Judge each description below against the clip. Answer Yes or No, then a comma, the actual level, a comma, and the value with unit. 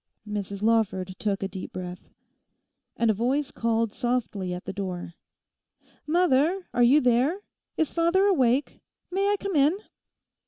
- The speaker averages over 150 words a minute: No, average, 145 wpm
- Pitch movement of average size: No, wide, 7.4 semitones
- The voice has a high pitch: Yes, high, 240 Hz